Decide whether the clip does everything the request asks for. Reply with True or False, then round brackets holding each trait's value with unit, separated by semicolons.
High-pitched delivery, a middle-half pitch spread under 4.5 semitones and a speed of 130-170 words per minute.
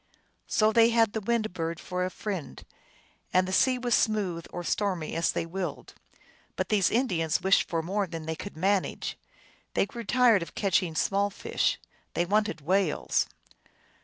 True (195 Hz; 4.1 semitones; 165 wpm)